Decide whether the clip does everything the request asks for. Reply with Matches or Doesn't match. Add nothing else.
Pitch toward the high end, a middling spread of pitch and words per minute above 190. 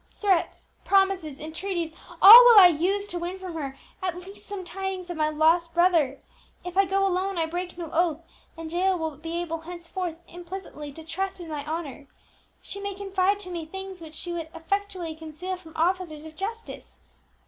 Doesn't match